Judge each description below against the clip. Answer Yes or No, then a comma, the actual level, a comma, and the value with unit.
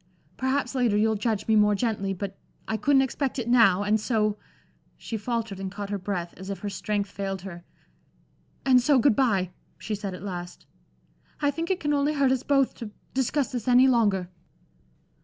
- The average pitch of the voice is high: Yes, high, 220 Hz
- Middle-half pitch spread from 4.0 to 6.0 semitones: Yes, average, 4.6 semitones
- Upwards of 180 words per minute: Yes, average, 190 wpm